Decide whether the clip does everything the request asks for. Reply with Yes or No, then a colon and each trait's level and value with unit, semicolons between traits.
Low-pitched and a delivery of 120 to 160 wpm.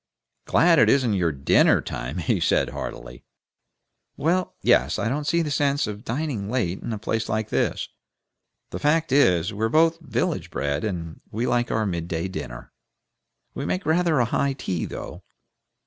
No: low, 115 Hz; average, 170 wpm